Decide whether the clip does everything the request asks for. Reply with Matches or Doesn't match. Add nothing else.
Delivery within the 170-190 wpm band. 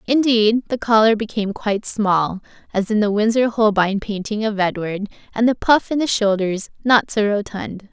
Matches